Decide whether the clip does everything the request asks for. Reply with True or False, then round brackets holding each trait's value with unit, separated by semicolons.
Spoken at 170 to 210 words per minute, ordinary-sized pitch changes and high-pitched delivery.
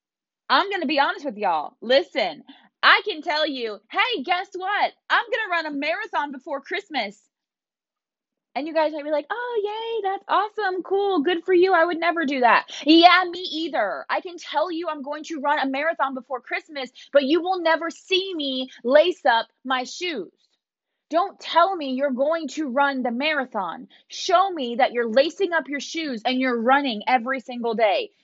True (190 wpm; 4.8 semitones; 310 Hz)